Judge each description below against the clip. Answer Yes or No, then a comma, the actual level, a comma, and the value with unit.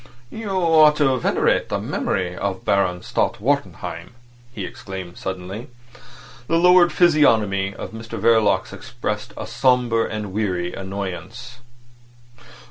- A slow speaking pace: Yes, slow, 120 wpm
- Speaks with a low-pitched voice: Yes, low, 110 Hz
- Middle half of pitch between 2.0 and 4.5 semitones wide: No, average, 5.3 semitones